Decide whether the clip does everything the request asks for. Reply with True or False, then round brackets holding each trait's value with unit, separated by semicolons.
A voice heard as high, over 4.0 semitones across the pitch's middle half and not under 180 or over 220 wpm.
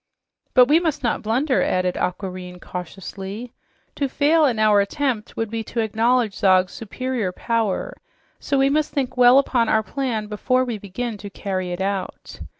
False (225 Hz; 4.7 semitones; 165 wpm)